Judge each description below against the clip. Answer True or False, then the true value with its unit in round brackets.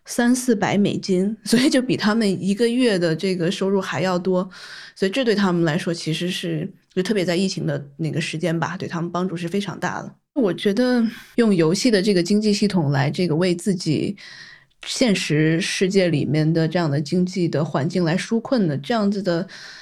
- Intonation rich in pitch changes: False (3.6 semitones)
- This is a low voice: False (185 Hz)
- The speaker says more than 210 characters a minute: True (295 characters per minute)